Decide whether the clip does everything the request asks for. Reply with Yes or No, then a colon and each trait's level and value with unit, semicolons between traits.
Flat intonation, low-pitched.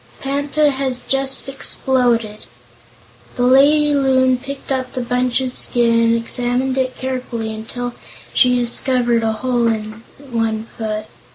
No: narrow, 2.3 semitones; very high, 250 Hz